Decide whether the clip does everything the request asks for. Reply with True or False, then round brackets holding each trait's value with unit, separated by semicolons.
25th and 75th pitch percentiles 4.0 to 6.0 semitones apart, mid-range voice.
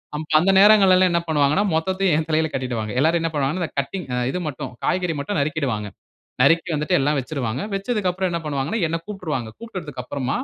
True (4.8 semitones; 160 Hz)